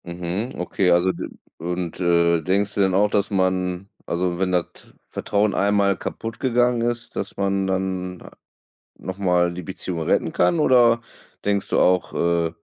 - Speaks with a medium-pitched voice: No, very low, 95 Hz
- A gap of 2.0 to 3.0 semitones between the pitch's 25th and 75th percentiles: Yes, narrow, 2.5 semitones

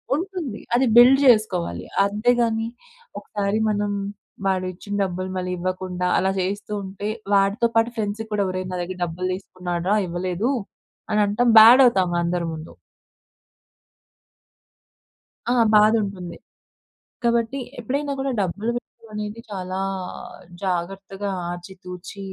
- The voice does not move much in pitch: No, average, 3.5 semitones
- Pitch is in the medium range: No, high, 200 Hz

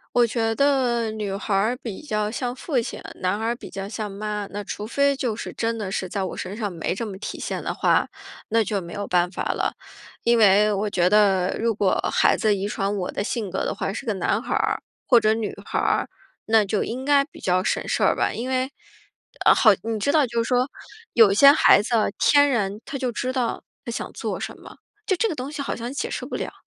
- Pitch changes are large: No, average, 3.6 semitones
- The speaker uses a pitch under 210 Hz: No, high, 220 Hz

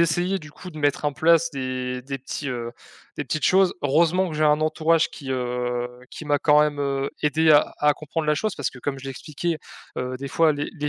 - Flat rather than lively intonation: No, average, 3.0 semitones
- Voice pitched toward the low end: No, medium, 150 Hz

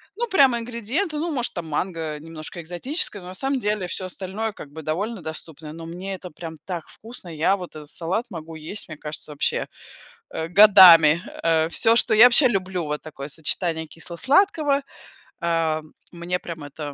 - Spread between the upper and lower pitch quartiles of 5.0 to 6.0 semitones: Yes, wide, 5.5 semitones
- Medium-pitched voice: Yes, medium, 175 Hz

